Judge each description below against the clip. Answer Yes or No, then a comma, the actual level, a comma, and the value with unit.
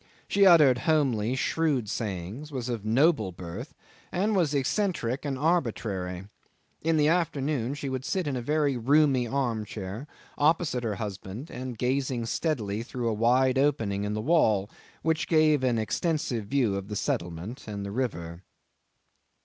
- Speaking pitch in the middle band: No, low, 125 Hz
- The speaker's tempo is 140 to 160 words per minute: Yes, average, 150 wpm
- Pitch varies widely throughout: Yes, wide, 5.8 semitones